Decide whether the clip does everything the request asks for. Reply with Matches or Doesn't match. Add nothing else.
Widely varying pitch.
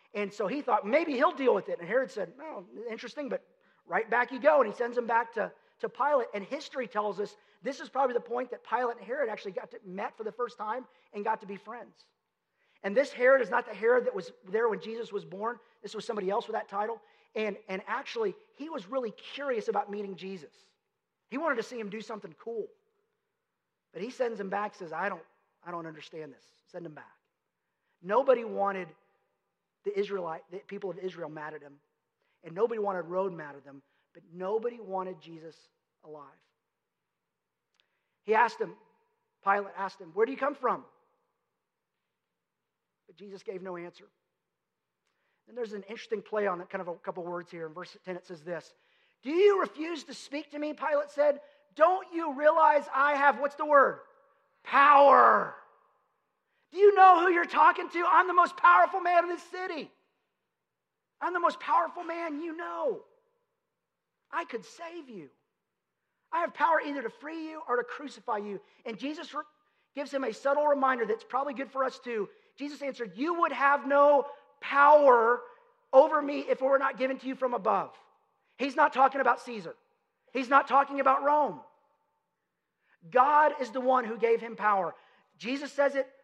Matches